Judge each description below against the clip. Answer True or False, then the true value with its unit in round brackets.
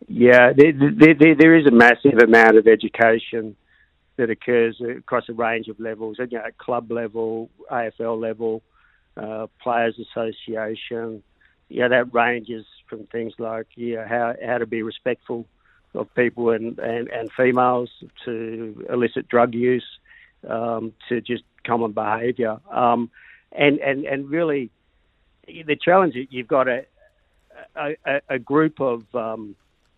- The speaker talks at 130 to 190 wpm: True (140 wpm)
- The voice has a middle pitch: False (115 Hz)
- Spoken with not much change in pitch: True (1.7 semitones)